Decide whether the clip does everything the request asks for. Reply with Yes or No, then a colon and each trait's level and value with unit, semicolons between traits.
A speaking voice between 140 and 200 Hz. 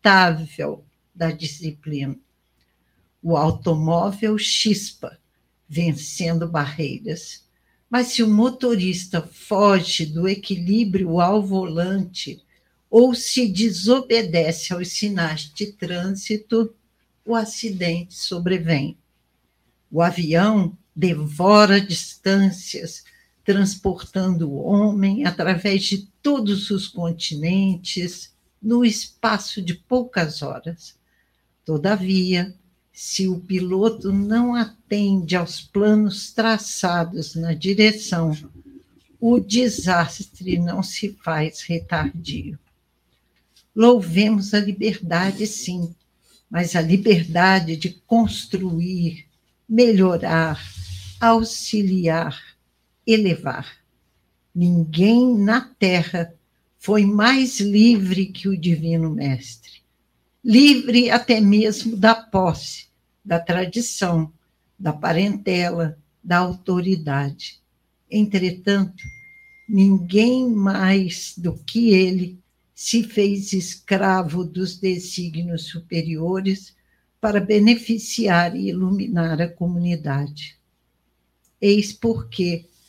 Yes: medium, 185 Hz